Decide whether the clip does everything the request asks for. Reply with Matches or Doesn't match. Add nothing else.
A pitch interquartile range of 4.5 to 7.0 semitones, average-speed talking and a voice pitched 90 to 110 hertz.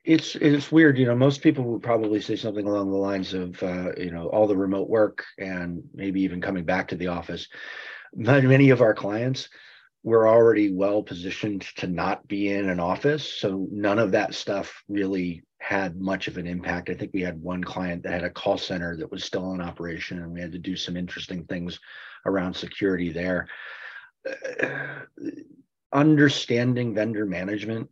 Matches